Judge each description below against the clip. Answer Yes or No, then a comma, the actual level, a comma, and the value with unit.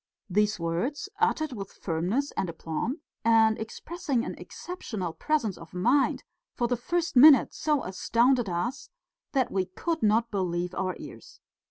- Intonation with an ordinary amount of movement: No, wide, 7.2 semitones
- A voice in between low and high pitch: No, high, 230 Hz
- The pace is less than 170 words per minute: Yes, average, 145 wpm